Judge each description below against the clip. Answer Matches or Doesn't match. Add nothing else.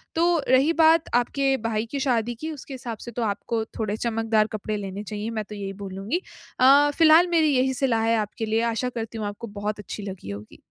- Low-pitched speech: Doesn't match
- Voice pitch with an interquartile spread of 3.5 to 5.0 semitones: Matches